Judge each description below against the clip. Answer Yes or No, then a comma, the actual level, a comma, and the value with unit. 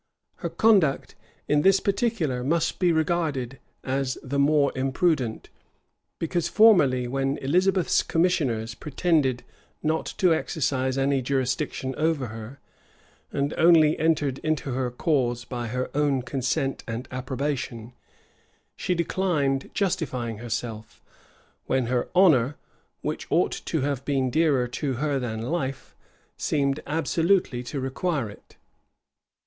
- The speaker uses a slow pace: Yes, slow, 120 wpm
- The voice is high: No, medium, 140 Hz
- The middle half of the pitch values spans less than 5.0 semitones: Yes, average, 4.1 semitones